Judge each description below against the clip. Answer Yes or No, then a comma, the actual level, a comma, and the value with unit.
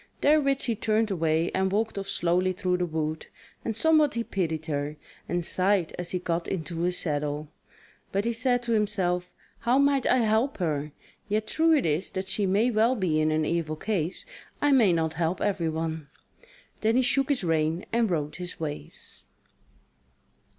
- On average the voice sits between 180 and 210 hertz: Yes, medium, 185 Hz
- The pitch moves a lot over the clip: Yes, wide, 5.8 semitones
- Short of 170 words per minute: No, average, 180 wpm